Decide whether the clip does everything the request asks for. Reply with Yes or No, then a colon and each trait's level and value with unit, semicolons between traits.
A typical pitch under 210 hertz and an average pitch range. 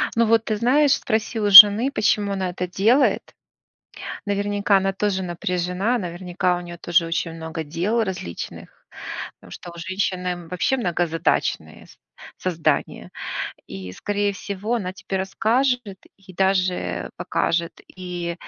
Yes: high, 190 Hz; average, 3.0 semitones